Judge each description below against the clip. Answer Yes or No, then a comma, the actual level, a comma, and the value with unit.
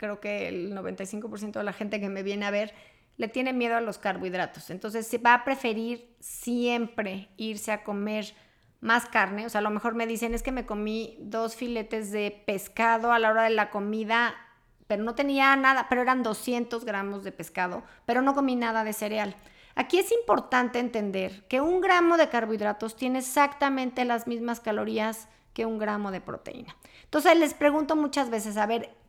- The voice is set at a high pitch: Yes, high, 225 Hz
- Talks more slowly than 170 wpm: No, fast, 190 wpm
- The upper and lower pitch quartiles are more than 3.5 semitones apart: No, average, 2.7 semitones